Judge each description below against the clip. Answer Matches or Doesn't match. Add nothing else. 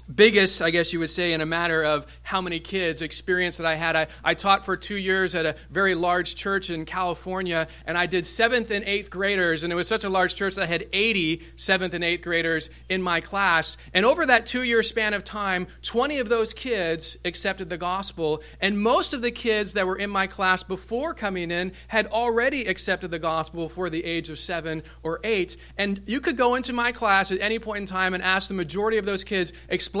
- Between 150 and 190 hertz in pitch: Matches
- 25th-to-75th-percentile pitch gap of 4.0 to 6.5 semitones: Doesn't match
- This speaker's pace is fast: Matches